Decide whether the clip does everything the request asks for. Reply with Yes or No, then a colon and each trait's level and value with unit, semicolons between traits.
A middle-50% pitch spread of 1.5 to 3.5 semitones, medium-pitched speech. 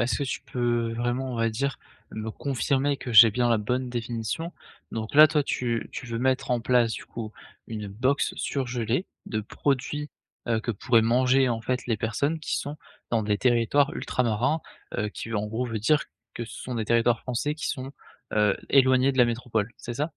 No: narrow, 2.6 semitones; low, 120 Hz